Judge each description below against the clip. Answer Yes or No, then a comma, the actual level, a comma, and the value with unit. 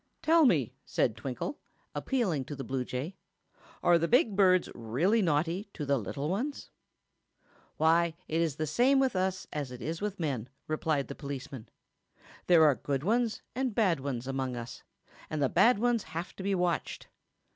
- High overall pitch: No, medium, 165 Hz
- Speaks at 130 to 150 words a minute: No, average, 170 wpm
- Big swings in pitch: Yes, wide, 6.4 semitones